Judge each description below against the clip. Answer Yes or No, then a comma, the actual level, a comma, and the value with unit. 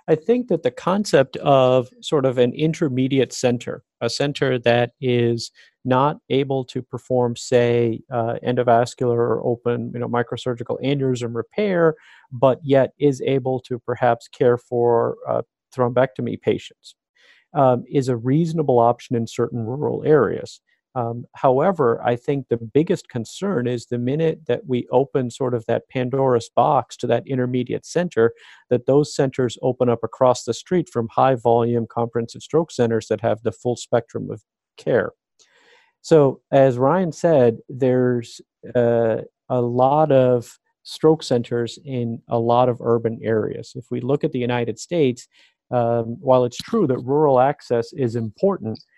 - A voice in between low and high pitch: No, low, 125 Hz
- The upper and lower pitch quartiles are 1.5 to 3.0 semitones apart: Yes, average, 2.7 semitones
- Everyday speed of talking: Yes, average, 155 wpm